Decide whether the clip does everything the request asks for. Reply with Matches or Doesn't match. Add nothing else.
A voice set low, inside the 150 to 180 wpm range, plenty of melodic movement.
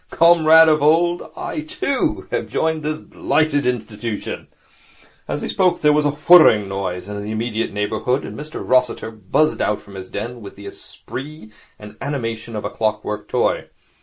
Matches